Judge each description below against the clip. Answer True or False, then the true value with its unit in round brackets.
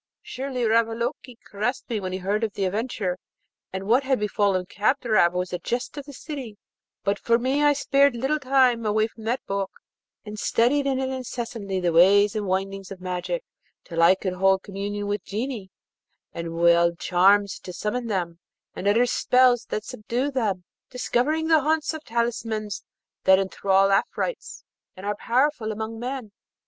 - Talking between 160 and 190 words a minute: True (170 wpm)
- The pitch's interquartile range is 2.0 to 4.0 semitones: False (4.6 semitones)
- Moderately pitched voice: False (215 Hz)